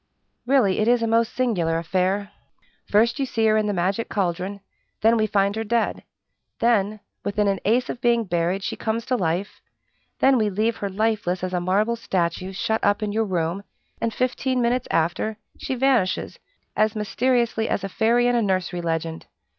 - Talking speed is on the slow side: No, average, 185 wpm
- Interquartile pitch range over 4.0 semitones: No, average, 3.7 semitones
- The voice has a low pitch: No, high, 210 Hz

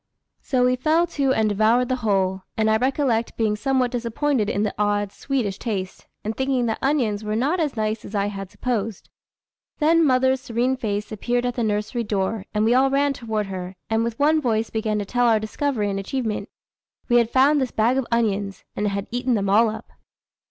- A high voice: Yes, high, 230 Hz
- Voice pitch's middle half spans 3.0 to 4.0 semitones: Yes, average, 3.7 semitones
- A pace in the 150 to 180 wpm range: No, fast, 205 wpm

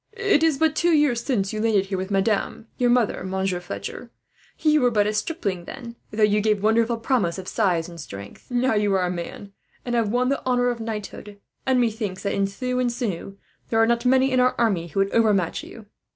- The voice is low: No, high, 220 Hz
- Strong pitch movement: No, average, 4.0 semitones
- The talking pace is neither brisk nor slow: No, fast, 225 wpm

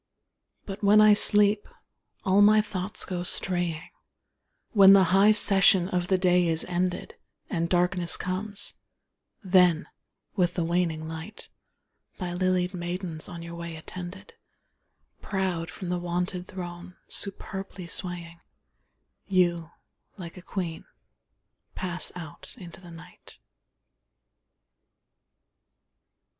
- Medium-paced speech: No, slow, 115 wpm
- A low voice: No, medium, 180 Hz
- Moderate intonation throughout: No, narrow, 1.8 semitones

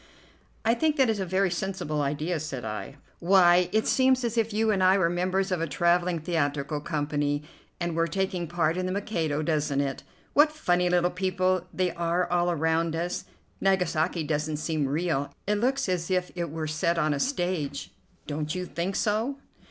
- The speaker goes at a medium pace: Yes, average, 185 wpm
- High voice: No, medium, 175 Hz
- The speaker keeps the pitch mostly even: No, average, 3.5 semitones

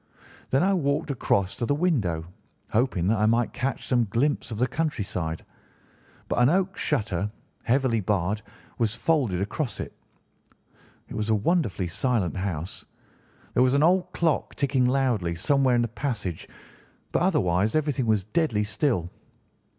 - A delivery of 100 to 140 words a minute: No, average, 155 wpm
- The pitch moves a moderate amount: No, wide, 6.0 semitones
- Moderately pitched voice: No, low, 120 Hz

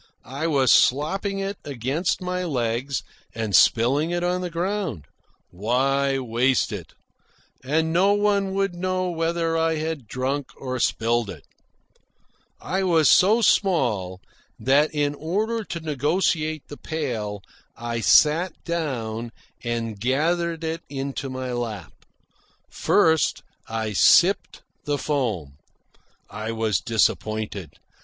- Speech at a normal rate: No, slow, 120 wpm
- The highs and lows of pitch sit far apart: Yes, wide, 6.4 semitones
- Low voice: No, medium, 145 Hz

